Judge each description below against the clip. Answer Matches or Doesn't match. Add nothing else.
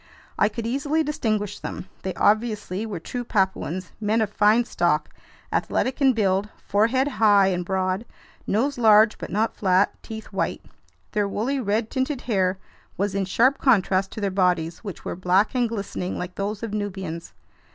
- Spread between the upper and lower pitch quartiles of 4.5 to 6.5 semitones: Doesn't match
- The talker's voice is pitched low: Doesn't match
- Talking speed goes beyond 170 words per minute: Doesn't match